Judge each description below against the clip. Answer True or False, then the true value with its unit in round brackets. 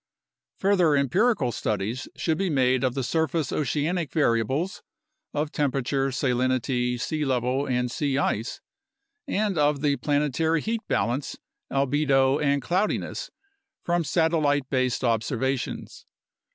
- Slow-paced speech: True (120 wpm)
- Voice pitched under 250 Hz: True (140 Hz)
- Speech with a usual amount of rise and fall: True (3.7 semitones)